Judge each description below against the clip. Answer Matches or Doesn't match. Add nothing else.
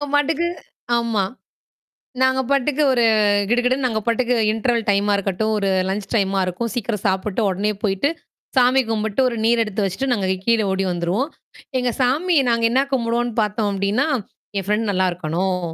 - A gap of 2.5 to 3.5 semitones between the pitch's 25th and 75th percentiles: Doesn't match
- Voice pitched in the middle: Doesn't match